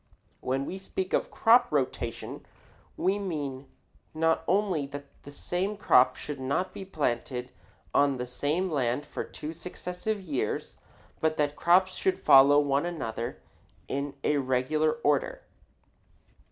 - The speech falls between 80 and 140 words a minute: Yes, slow, 135 wpm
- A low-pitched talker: No, medium, 150 Hz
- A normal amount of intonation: Yes, average, 5.0 semitones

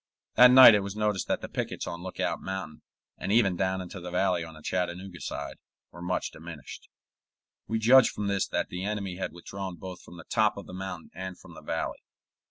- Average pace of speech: No, fast, 210 wpm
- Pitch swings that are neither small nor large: No, narrow, 2.3 semitones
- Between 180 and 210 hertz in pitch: No, very low, 95 Hz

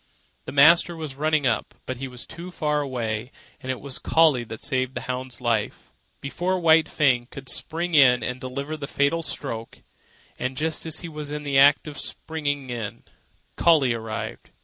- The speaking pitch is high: No, medium, 140 Hz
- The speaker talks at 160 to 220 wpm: Yes, average, 175 wpm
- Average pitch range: Yes, average, 3.6 semitones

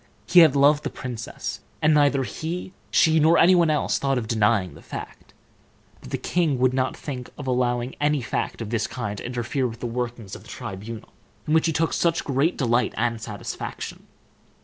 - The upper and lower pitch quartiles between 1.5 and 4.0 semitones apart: No, average, 4.5 semitones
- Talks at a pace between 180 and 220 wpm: Yes, average, 195 wpm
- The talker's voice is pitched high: No, low, 130 Hz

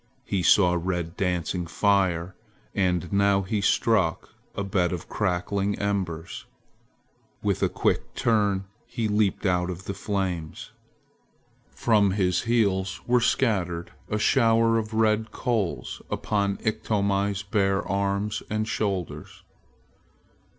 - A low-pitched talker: Yes, low, 100 Hz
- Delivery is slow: Yes, slow, 115 wpm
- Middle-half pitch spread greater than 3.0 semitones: No, average, 2.7 semitones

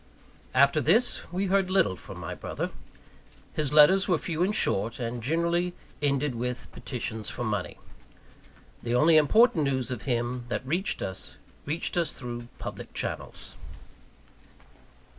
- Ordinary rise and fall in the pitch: No, wide, 6.1 semitones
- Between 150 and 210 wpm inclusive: No, average, 140 wpm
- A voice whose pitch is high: No, medium, 140 Hz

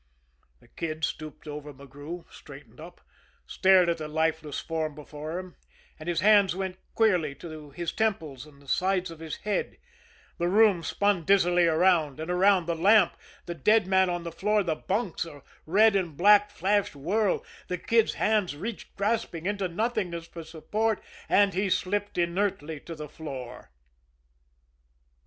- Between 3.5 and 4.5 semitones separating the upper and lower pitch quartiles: Yes, average, 4.1 semitones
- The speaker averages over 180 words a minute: No, average, 160 wpm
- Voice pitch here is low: No, medium, 175 Hz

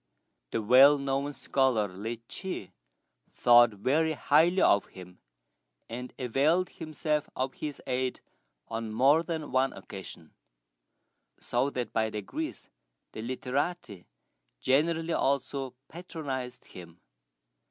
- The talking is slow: Yes, slow, 110 wpm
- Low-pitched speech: Yes, low, 130 Hz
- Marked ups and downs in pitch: No, average, 4.8 semitones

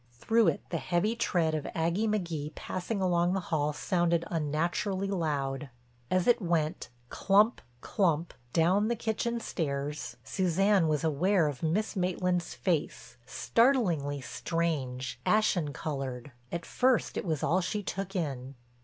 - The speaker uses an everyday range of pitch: Yes, average, 4.5 semitones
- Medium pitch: Yes, medium, 170 Hz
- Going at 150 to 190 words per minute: No, slow, 135 wpm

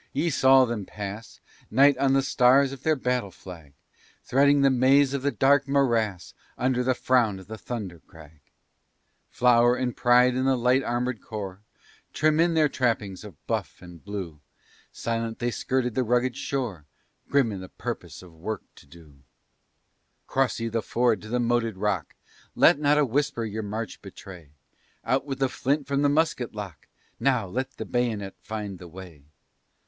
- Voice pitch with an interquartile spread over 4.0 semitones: Yes, average, 4.7 semitones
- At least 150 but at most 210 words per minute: Yes, average, 175 wpm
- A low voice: Yes, low, 120 Hz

